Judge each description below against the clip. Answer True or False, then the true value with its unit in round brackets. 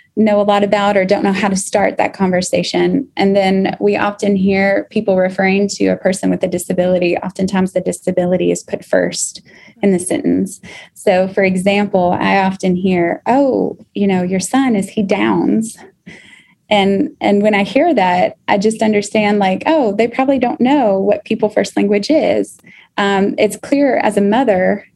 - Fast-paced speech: False (180 wpm)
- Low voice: False (200 Hz)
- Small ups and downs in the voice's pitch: True (2.1 semitones)